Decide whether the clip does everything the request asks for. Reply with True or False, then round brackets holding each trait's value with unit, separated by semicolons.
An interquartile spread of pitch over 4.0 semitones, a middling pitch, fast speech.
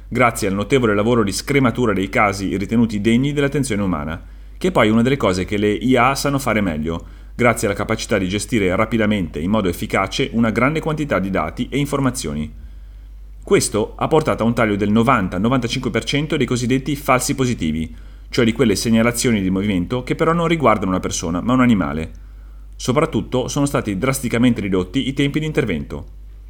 False (5.4 semitones; 115 Hz; 175 wpm)